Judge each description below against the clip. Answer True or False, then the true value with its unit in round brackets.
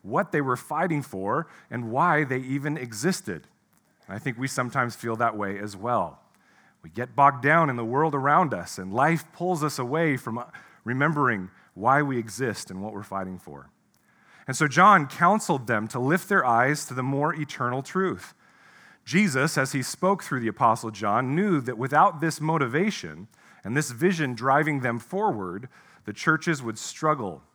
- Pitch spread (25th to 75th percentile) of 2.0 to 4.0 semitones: False (5.2 semitones)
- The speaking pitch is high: False (135 Hz)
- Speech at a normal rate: True (175 wpm)